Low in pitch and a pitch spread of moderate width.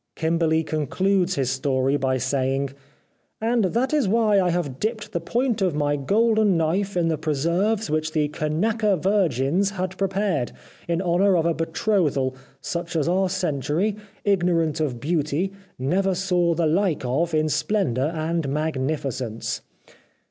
No: medium, 170 Hz; average, 4.8 semitones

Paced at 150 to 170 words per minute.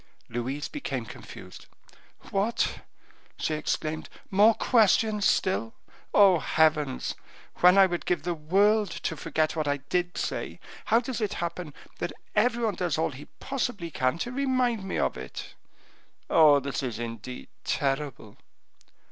No: average, 140 wpm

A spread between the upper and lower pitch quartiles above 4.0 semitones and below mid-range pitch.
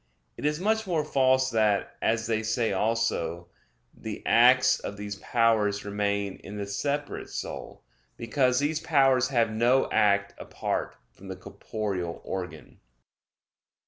Yes: average, 4.4 semitones; low, 115 Hz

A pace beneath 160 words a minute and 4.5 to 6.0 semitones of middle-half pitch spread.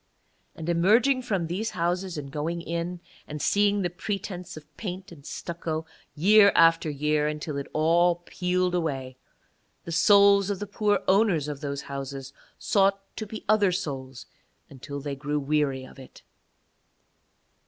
Yes: average, 150 wpm; average, 5.0 semitones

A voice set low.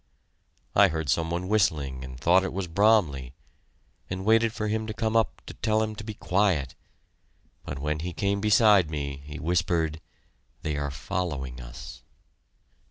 Yes: very low, 85 Hz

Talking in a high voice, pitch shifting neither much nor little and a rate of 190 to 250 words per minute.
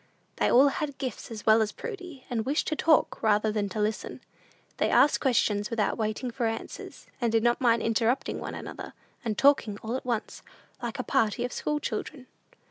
Yes: high, 235 Hz; average, 3.5 semitones; average, 195 wpm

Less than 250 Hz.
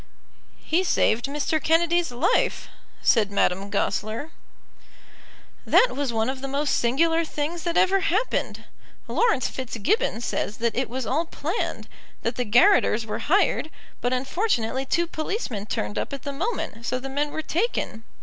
No: very high, 275 Hz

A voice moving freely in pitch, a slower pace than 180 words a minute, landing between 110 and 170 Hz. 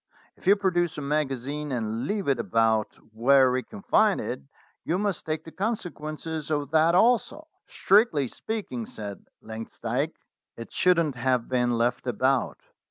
Yes: wide, 6.1 semitones; average, 155 wpm; medium, 140 Hz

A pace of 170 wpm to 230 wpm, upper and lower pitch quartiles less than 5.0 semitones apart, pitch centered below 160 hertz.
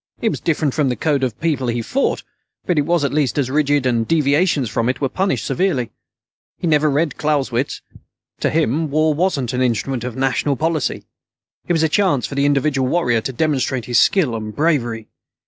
Yes: average, 200 wpm; average, 3.8 semitones; medium, 140 Hz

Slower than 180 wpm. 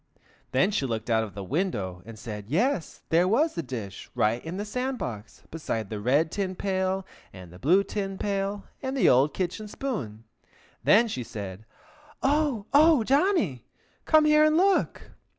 Yes: average, 170 wpm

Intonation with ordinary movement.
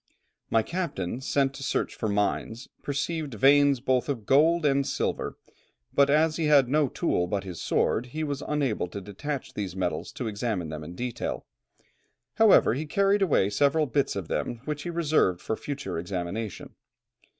No: wide, 6.5 semitones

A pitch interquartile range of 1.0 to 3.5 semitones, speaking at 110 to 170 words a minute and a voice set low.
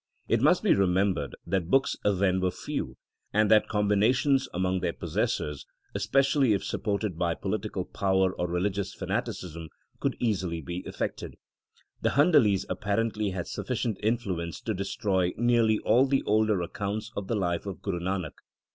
Yes: average, 3.0 semitones; average, 155 wpm; low, 100 Hz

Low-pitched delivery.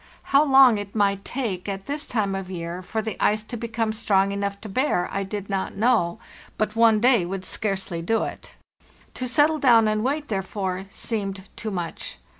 No: high, 210 Hz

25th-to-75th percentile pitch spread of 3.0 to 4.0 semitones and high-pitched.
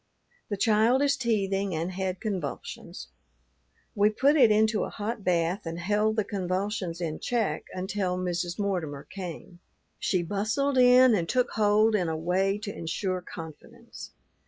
Yes: average, 3.5 semitones; high, 195 Hz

